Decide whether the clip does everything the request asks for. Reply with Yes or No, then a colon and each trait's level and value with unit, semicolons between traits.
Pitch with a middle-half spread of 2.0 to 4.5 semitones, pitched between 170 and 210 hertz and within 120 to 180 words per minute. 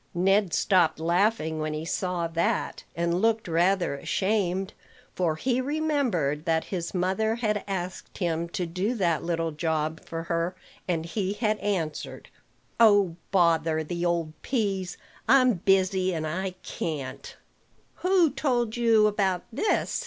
Yes: average, 4.2 semitones; medium, 185 Hz; average, 140 wpm